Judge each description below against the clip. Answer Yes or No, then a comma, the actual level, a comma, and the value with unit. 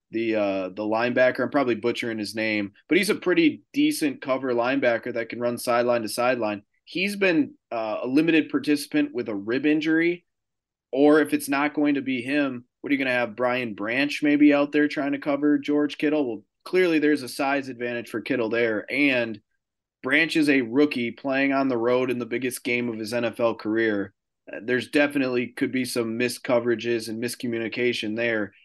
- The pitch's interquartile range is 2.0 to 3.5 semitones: No, average, 3.9 semitones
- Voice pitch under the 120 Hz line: No, low, 125 Hz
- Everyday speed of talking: Yes, average, 195 wpm